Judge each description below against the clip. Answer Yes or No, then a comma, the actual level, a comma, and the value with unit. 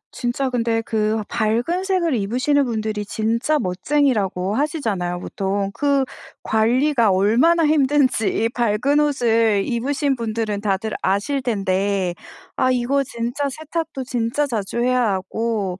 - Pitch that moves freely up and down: No, average, 4.9 semitones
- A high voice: Yes, high, 235 Hz